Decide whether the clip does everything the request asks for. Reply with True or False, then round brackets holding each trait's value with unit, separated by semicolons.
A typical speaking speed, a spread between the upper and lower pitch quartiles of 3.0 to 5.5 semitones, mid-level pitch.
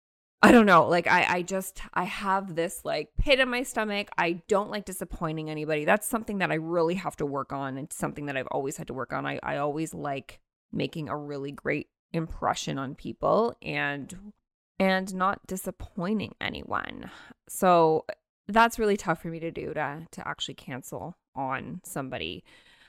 True (180 wpm; 4.3 semitones; 175 Hz)